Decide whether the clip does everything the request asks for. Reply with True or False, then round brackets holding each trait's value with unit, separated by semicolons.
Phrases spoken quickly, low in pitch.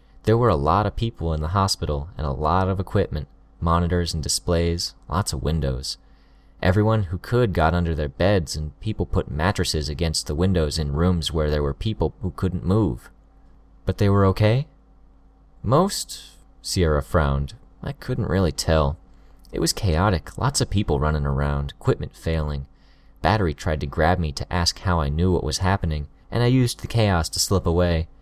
False (180 wpm; 85 Hz)